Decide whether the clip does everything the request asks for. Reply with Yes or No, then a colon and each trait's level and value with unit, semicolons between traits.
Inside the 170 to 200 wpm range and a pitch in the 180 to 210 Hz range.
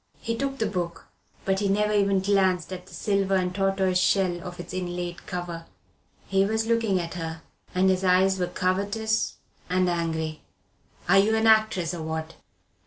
Yes: average, 175 wpm; medium, 185 Hz